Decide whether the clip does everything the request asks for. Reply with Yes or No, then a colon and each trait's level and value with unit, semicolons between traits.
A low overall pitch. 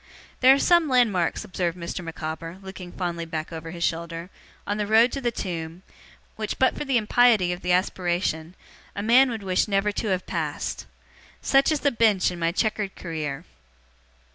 No: medium, 185 Hz